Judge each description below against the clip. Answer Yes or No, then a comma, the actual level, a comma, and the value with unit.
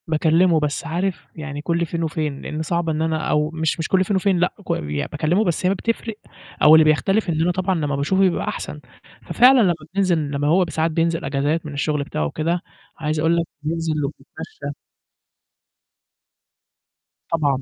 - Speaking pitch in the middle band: Yes, medium, 160 Hz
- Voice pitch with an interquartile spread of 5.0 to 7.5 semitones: No, narrow, 2.6 semitones